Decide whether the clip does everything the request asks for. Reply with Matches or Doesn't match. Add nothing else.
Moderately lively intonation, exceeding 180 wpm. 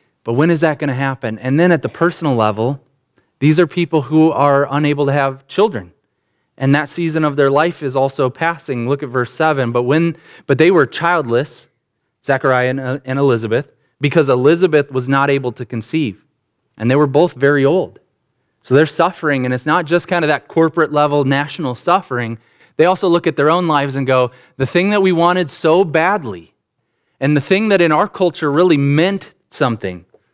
Matches